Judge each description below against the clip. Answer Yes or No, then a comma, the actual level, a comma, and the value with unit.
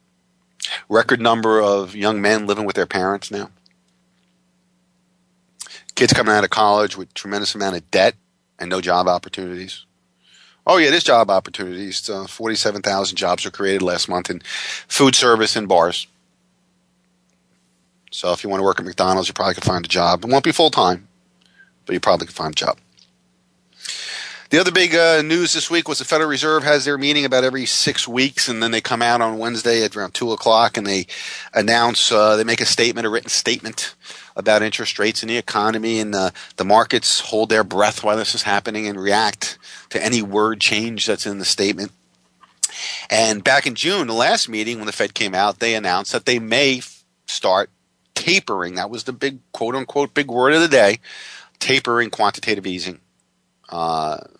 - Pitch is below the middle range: Yes, low, 105 Hz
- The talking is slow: No, average, 190 wpm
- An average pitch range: Yes, average, 4.7 semitones